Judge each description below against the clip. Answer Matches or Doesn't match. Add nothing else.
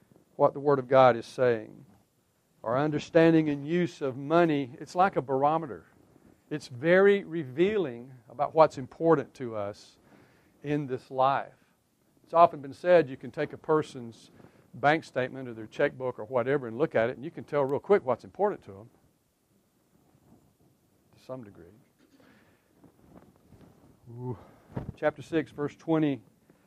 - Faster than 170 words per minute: Doesn't match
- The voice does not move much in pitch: Doesn't match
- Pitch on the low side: Doesn't match